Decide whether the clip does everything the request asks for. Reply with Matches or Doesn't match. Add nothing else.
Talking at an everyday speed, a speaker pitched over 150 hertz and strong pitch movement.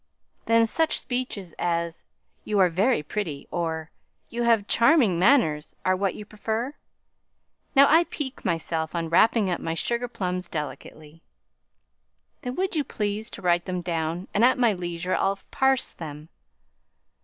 Matches